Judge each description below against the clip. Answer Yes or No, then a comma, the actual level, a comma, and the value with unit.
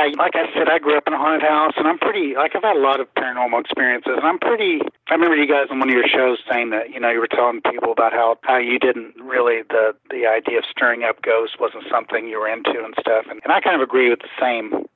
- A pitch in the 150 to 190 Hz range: No, low, 135 Hz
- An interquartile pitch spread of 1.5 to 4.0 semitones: No, average, 4.9 semitones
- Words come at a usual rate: No, fast, 280 wpm